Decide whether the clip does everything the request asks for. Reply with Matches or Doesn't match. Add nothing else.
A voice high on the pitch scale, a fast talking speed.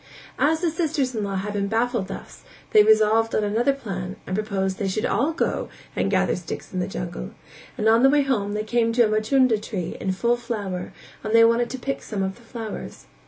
Matches